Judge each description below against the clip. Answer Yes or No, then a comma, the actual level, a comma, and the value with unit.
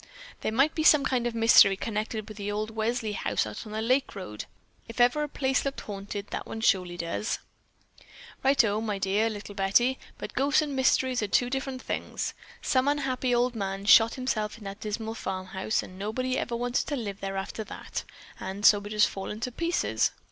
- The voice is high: Yes, high, 220 Hz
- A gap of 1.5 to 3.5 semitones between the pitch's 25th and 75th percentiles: No, average, 4.0 semitones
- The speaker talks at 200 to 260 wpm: Yes, fast, 205 wpm